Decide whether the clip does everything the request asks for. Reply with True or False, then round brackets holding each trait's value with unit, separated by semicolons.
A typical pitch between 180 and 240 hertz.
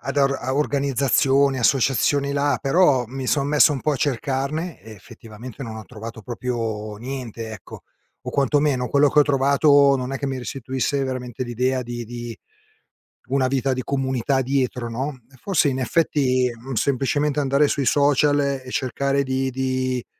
False (135 Hz)